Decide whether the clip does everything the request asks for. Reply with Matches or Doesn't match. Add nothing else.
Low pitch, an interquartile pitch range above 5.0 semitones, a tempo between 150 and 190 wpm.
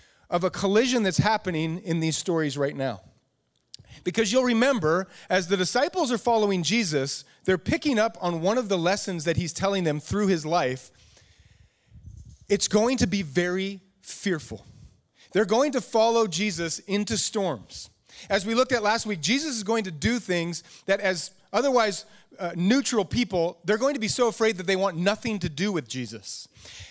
Doesn't match